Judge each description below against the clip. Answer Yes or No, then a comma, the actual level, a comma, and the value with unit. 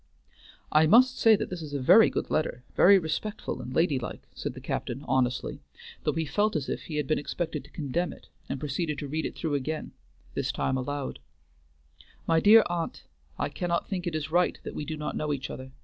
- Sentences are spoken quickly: Yes, fast, 215 wpm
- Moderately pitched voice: Yes, medium, 155 Hz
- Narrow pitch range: No, average, 3.8 semitones